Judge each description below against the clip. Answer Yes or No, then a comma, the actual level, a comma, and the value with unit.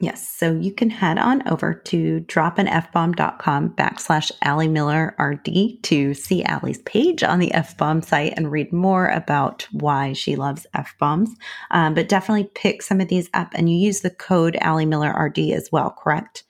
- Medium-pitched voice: Yes, medium, 170 Hz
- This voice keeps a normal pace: Yes, average, 190 wpm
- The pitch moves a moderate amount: Yes, average, 4.0 semitones